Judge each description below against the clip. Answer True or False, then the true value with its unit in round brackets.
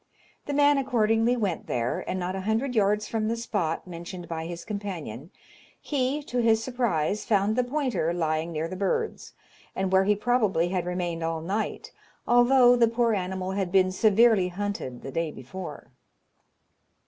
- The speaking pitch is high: True (195 Hz)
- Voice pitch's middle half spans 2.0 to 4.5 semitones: False (5.1 semitones)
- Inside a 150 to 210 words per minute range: True (165 wpm)